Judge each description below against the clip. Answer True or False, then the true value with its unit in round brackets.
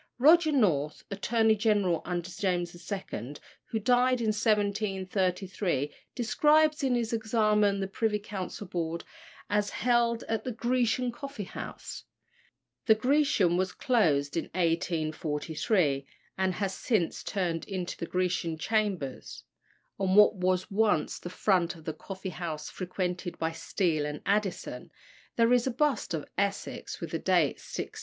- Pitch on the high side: True (195 Hz)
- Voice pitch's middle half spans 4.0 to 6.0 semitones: True (4.3 semitones)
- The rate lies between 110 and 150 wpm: True (140 wpm)